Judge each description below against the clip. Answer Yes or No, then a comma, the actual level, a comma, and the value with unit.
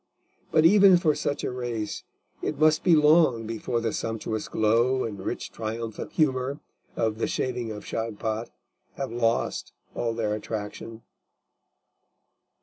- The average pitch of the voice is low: Yes, low, 115 Hz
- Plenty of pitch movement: No, average, 3.9 semitones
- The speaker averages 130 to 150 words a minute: Yes, slow, 135 wpm